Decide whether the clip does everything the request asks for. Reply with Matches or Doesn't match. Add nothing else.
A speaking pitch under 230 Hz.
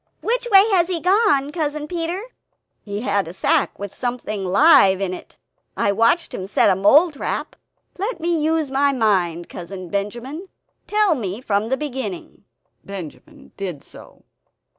Doesn't match